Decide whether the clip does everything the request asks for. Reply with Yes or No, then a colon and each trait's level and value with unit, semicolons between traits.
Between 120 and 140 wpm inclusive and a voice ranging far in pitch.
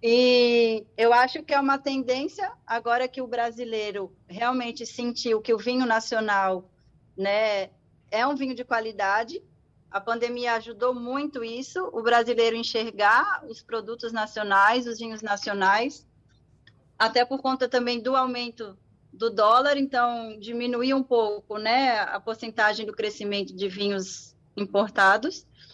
No: average, 135 wpm; average, 2.7 semitones